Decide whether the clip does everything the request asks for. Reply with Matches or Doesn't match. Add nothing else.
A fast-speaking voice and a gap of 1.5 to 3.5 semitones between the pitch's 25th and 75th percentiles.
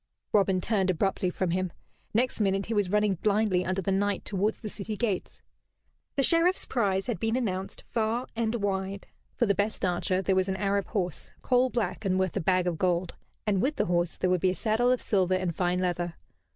Matches